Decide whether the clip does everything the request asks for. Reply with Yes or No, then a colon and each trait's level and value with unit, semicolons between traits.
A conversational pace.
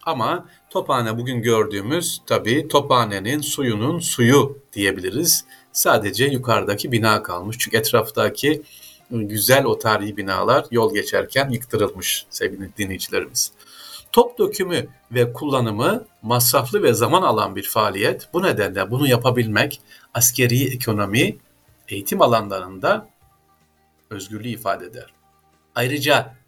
Yes: average, 105 wpm